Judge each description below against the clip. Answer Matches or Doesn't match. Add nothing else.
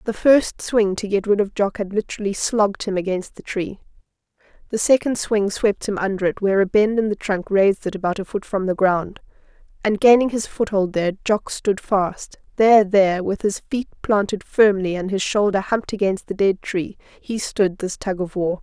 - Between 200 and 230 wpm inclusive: Matches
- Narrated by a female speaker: Matches